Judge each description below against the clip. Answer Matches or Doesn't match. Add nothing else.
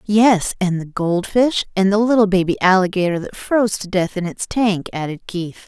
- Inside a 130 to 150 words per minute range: Doesn't match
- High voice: Matches